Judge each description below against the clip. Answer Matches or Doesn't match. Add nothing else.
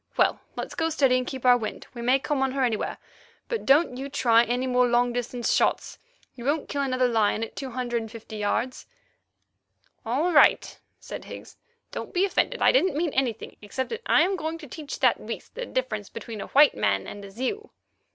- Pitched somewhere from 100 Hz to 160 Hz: Doesn't match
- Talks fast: Matches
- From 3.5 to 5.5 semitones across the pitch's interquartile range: Matches